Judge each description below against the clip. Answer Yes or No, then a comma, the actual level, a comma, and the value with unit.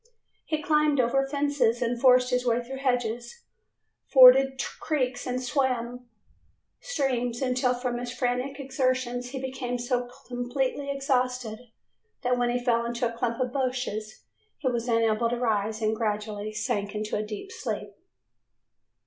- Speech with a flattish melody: Yes, narrow, 1.9 semitones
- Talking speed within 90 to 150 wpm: Yes, average, 145 wpm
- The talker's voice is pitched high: Yes, high, 245 Hz